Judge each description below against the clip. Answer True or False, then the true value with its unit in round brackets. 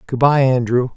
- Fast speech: False (190 wpm)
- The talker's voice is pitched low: True (130 Hz)